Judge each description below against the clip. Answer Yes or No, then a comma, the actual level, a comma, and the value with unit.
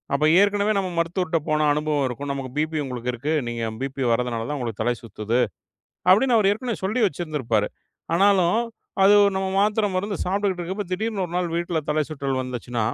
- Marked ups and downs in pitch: Yes, wide, 7.2 semitones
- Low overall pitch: No, medium, 155 Hz